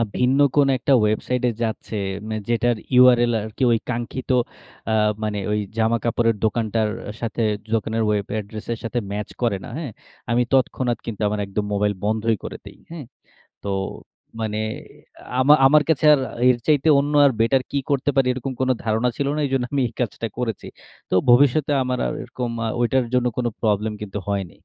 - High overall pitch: No, low, 120 Hz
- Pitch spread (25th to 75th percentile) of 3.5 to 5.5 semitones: No, average, 3.0 semitones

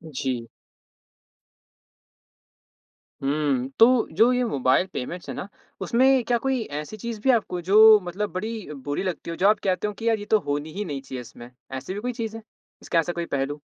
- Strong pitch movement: Yes, wide, 7.4 semitones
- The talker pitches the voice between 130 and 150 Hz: No, medium, 185 Hz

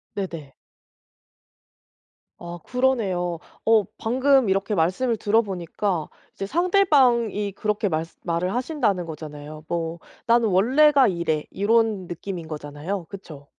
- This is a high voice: Yes, high, 195 Hz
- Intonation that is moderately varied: No, wide, 5.7 semitones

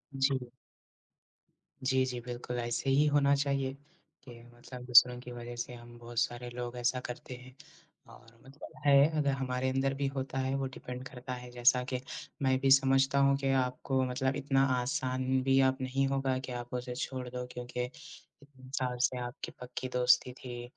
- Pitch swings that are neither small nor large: No, narrow, 1.5 semitones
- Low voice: Yes, low, 130 Hz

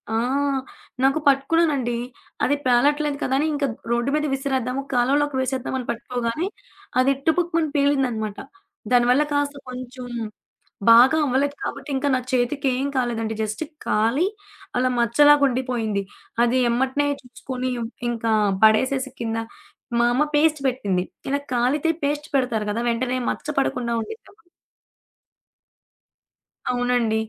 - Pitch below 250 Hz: No, very high, 255 Hz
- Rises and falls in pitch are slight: No, average, 3.1 semitones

